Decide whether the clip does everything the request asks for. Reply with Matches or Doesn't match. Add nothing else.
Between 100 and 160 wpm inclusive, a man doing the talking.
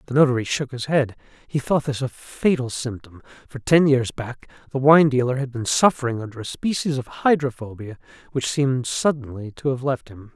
Doesn't match